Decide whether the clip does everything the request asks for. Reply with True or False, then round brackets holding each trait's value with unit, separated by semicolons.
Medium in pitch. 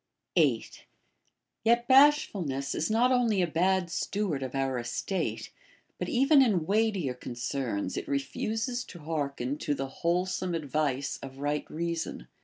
True (165 Hz)